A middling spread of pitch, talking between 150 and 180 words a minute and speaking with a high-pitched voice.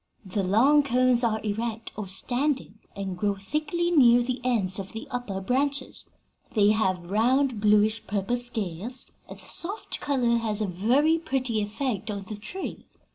Yes: average, 4.1 semitones; average, 160 wpm; high, 230 Hz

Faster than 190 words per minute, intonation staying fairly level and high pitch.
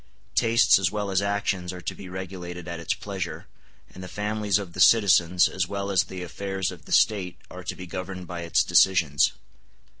No: average, 200 wpm; narrow, 1.9 semitones; very low, 90 Hz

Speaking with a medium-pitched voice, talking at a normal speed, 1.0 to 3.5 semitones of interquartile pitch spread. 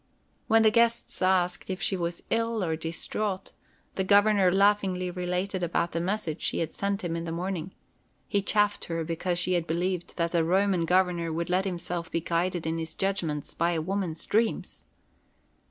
Yes: medium, 180 Hz; average, 180 wpm; average, 2.7 semitones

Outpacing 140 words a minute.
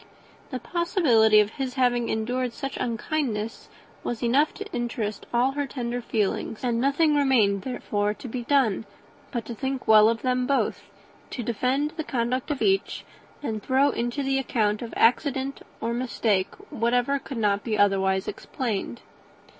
Yes: average, 160 wpm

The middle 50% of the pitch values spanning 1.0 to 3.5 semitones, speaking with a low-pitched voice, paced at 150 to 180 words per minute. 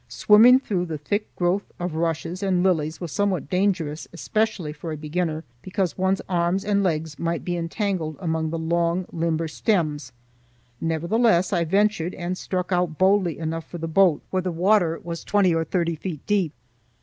No: average, 2.9 semitones; medium, 175 Hz; average, 175 wpm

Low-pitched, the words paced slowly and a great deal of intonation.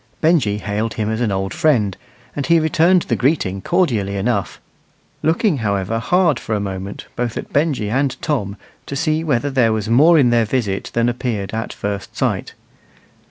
No: low, 120 Hz; average, 175 wpm; wide, 6.6 semitones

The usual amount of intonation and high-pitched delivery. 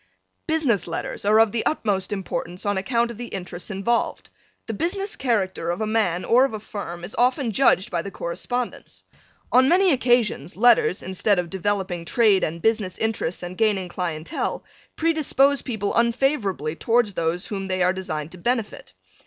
Yes: average, 4.8 semitones; high, 205 Hz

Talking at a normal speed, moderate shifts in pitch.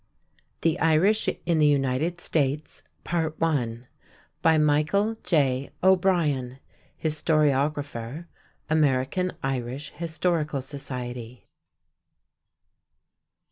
No: slow, 65 wpm; average, 3.8 semitones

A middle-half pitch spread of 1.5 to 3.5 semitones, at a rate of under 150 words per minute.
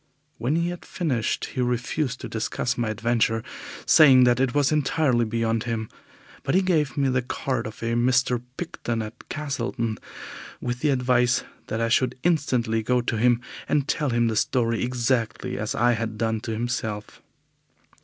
No: narrow, 2.4 semitones; average, 170 wpm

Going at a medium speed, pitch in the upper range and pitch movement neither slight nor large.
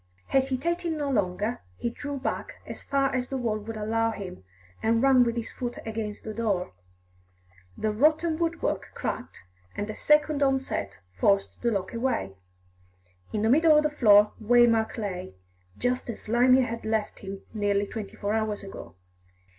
Yes: average, 160 wpm; high, 230 Hz; average, 4.2 semitones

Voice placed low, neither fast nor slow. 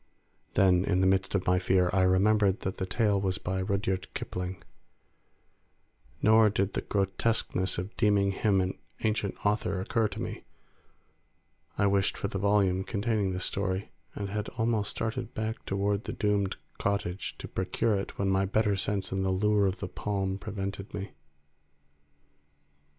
Yes: low, 100 Hz; average, 160 wpm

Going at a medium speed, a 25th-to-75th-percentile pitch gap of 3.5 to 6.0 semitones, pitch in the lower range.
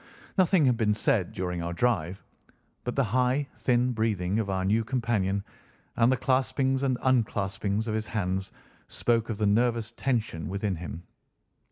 Yes: average, 160 wpm; average, 4.2 semitones; low, 110 Hz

